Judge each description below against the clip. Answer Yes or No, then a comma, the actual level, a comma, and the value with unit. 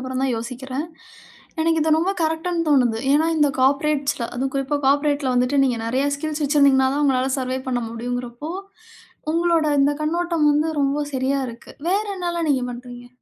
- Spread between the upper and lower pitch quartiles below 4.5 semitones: Yes, average, 3.2 semitones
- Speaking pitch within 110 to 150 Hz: No, very high, 280 Hz